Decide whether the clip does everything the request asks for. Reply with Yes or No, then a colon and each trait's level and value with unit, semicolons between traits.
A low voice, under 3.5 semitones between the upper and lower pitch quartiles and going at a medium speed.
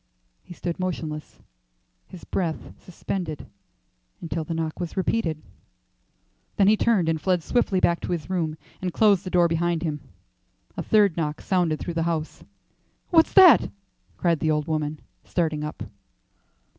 No: medium, 170 Hz; average, 2.8 semitones; average, 150 wpm